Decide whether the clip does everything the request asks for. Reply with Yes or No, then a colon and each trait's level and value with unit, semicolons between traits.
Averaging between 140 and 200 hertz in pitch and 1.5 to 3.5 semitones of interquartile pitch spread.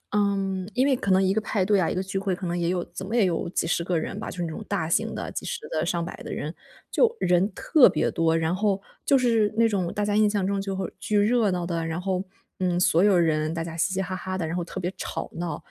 Yes: medium, 185 Hz; average, 3.1 semitones